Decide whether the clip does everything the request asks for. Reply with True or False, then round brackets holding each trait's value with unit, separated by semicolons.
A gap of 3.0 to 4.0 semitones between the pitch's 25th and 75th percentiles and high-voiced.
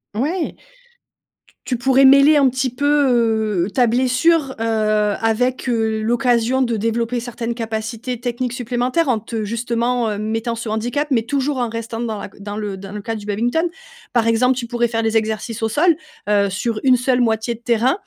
False (2.5 semitones; 235 Hz)